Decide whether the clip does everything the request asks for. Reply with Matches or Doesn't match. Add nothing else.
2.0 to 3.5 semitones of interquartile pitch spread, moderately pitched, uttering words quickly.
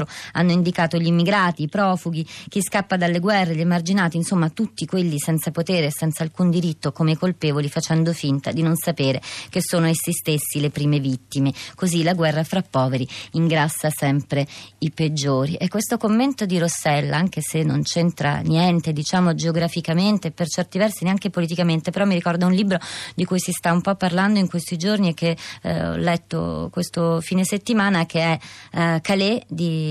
Matches